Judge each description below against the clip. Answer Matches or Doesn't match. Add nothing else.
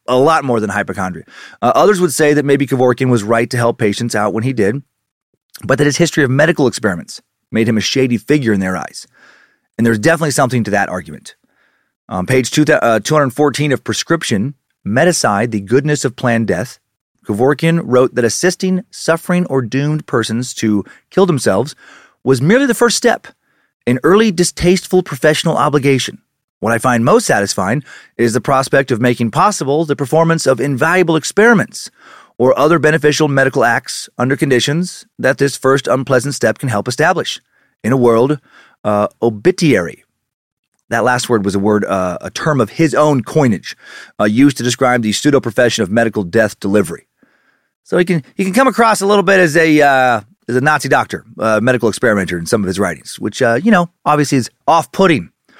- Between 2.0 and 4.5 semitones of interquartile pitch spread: Doesn't match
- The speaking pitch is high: Doesn't match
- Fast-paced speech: Doesn't match